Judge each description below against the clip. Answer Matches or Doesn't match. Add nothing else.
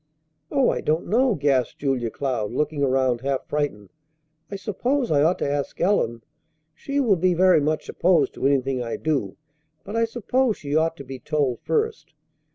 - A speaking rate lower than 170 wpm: Doesn't match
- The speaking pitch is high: Doesn't match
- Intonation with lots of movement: Matches